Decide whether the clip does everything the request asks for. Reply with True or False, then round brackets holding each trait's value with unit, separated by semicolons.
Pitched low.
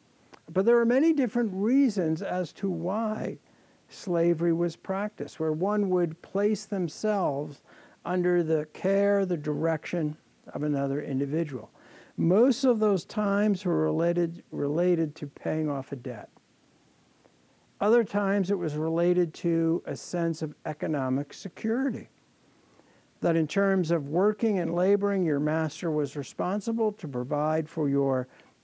False (175 Hz)